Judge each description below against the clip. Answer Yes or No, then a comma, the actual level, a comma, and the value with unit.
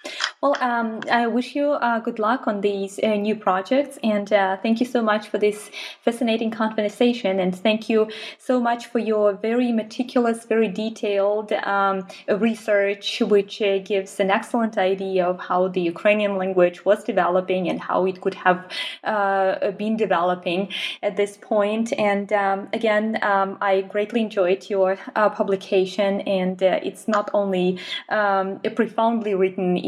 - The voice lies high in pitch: Yes, high, 205 Hz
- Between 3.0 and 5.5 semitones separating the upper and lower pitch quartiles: No, narrow, 2.6 semitones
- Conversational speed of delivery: Yes, average, 160 wpm